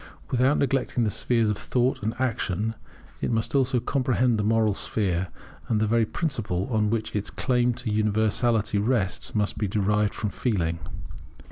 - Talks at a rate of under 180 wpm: Yes, average, 160 wpm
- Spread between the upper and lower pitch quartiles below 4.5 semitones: Yes, average, 2.8 semitones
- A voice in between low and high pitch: No, low, 110 Hz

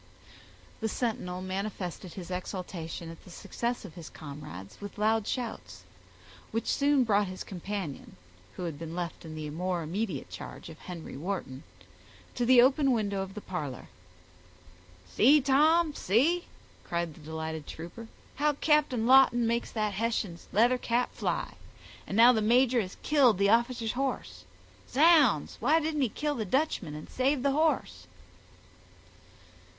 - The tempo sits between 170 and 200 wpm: No, average, 145 wpm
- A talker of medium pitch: No, high, 210 Hz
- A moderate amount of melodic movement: No, wide, 6.8 semitones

